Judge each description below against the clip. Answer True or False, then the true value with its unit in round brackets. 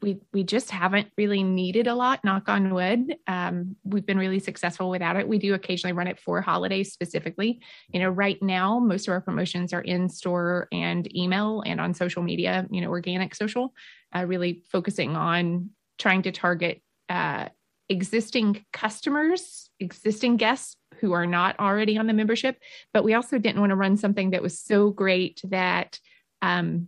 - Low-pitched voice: False (195 Hz)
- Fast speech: False (180 wpm)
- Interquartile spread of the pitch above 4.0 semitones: False (3.0 semitones)